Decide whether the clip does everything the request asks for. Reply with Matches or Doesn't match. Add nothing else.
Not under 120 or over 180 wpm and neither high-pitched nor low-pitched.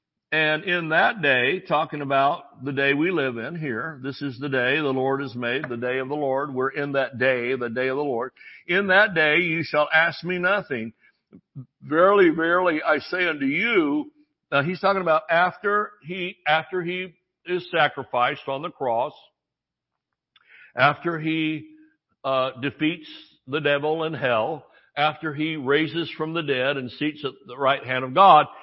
Matches